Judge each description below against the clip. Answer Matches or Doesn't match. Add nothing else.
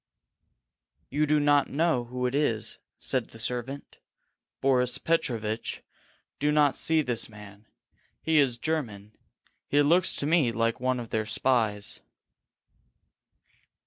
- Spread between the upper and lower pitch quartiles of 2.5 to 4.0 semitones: Doesn't match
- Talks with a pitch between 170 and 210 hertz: Doesn't match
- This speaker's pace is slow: Matches